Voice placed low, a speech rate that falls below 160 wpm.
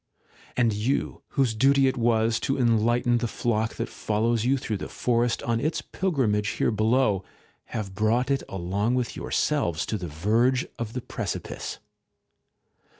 Yes: low, 115 Hz; average, 150 wpm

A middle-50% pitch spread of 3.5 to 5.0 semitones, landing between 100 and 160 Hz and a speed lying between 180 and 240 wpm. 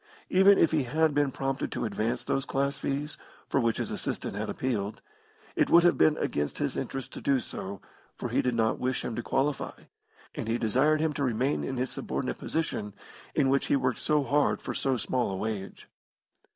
Yes: average, 4.0 semitones; low, 135 Hz; fast, 205 wpm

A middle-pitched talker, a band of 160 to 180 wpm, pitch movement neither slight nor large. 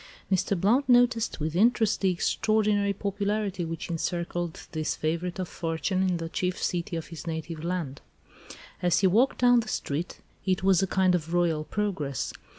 Yes: medium, 180 Hz; average, 165 wpm; average, 3.5 semitones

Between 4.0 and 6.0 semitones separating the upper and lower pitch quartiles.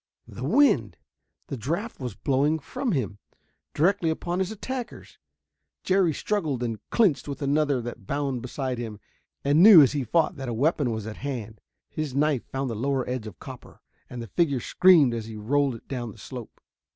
Yes: average, 4.9 semitones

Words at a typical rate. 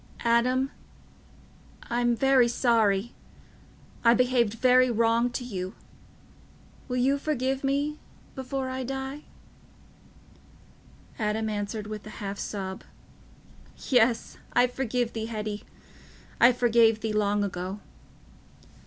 No: slow, 105 wpm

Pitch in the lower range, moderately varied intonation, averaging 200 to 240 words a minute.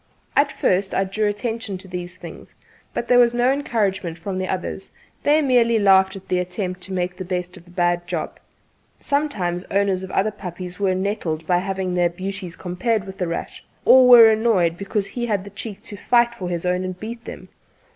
No: high, 190 Hz; average, 3.6 semitones; fast, 205 wpm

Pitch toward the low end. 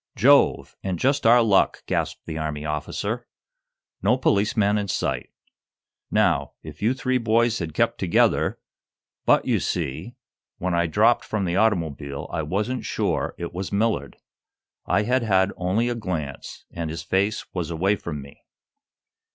Yes: very low, 95 Hz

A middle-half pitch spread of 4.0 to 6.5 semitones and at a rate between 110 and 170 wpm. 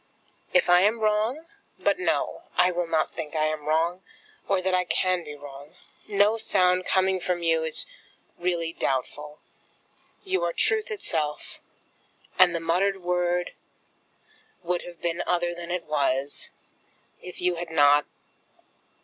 No: narrow, 2.6 semitones; average, 145 wpm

